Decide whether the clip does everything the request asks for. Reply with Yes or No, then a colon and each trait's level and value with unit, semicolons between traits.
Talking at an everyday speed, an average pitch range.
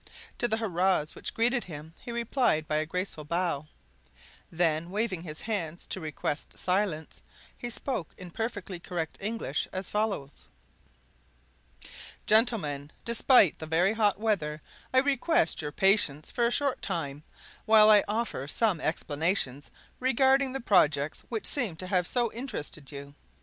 No: average, 145 wpm; wide, 6.5 semitones